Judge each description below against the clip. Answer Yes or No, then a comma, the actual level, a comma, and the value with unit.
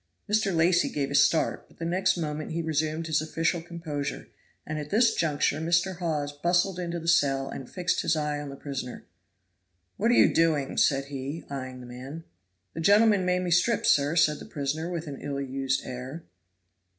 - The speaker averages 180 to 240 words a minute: Yes, average, 190 wpm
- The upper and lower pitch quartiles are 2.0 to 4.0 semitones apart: Yes, average, 3.5 semitones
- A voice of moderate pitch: Yes, medium, 155 Hz